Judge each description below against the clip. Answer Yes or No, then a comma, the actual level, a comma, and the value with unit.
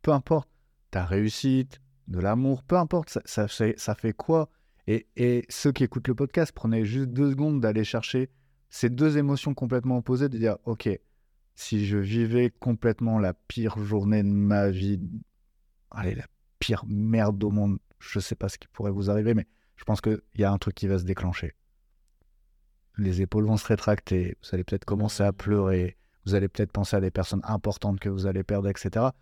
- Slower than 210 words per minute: Yes, average, 195 wpm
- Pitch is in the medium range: No, low, 105 Hz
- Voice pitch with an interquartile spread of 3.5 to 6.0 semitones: Yes, average, 3.9 semitones